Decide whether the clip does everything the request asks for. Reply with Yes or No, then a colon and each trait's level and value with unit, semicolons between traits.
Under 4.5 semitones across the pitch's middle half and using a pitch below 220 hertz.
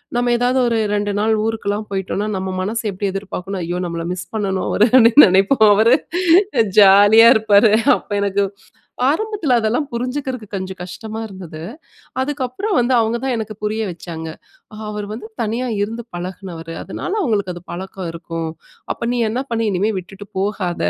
Yes: average, 3.5 semitones; high, 210 Hz